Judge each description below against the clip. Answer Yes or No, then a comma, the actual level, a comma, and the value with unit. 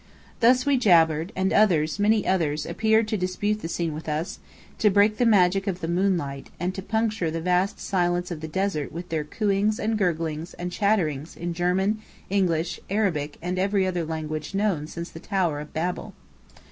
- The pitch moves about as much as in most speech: Yes, average, 3.8 semitones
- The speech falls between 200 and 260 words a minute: No, average, 185 wpm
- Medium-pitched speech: Yes, medium, 180 Hz